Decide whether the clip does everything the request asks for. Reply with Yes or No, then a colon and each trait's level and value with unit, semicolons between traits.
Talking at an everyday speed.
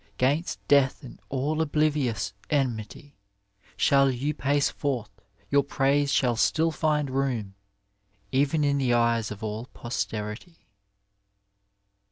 No: slow, 115 wpm